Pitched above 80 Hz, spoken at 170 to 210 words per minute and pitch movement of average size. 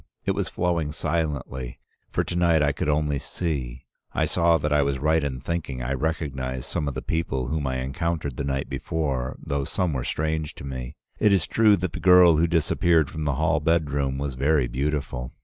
No: very low, 75 Hz; average, 200 wpm; average, 3.5 semitones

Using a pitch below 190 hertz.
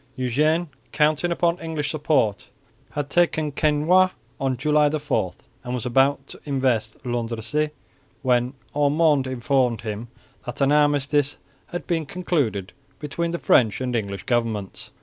Yes: medium, 140 Hz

